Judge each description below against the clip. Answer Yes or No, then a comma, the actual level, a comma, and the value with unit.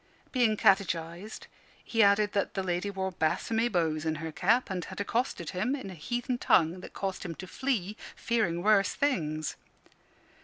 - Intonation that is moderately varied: Yes, average, 4.5 semitones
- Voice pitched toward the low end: No, high, 195 Hz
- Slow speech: No, average, 165 wpm